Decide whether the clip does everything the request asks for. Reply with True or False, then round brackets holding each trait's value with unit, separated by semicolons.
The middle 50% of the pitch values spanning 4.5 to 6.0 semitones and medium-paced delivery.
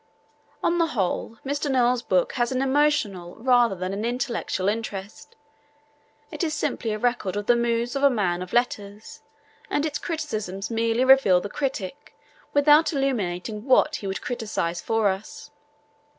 True (5.2 semitones; 155 wpm)